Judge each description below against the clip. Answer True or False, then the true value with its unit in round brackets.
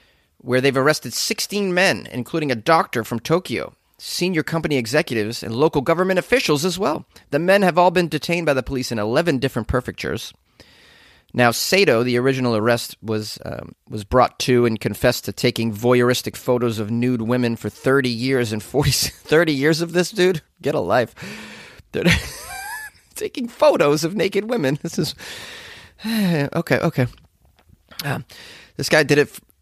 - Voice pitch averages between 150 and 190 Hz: False (135 Hz)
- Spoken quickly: False (160 wpm)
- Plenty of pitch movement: True (6.2 semitones)